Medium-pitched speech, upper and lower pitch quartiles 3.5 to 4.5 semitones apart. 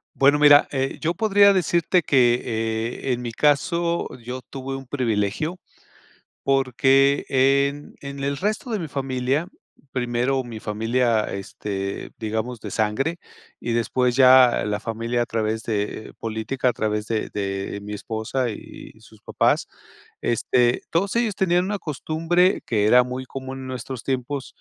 No: low, 130 Hz; average, 4.1 semitones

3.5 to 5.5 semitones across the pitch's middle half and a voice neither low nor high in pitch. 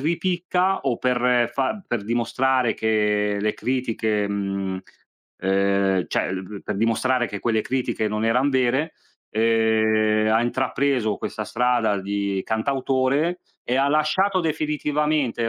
No: average, 4.2 semitones; low, 120 Hz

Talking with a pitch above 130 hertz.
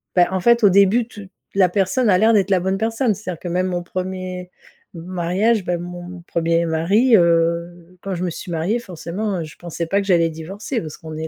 Yes: medium, 185 Hz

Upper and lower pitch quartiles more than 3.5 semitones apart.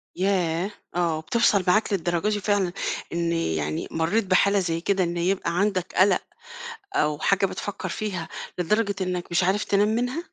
No: average, 3.0 semitones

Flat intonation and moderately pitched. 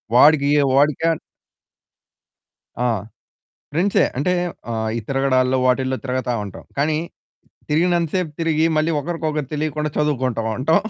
No: average, 3.4 semitones; medium, 150 Hz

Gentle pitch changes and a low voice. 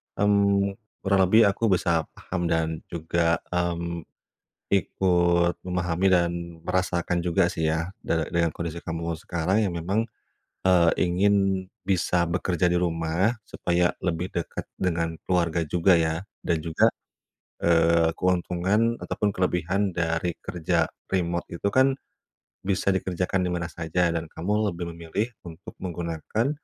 Yes: narrow, 2.0 semitones; very low, 85 Hz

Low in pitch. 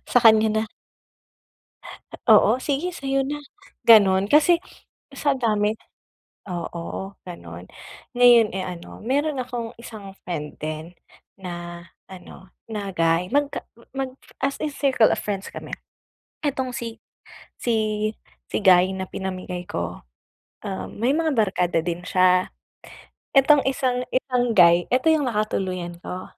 No: high, 215 Hz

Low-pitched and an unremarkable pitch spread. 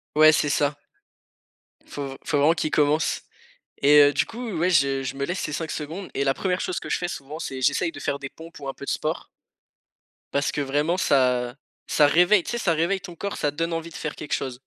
No: medium, 150 Hz; average, 3.3 semitones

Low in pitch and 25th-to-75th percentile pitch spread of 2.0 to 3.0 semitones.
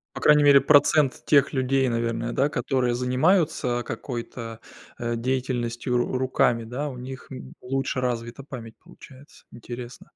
Yes: low, 125 Hz; narrow, 2.4 semitones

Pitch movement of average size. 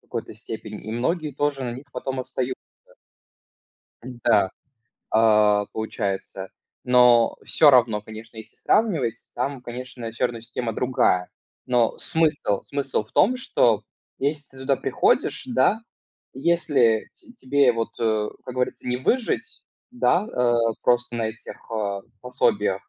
Yes: average, 3.3 semitones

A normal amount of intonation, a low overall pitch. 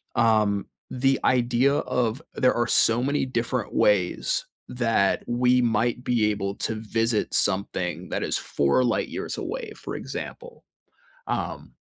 Yes: average, 3.1 semitones; low, 120 Hz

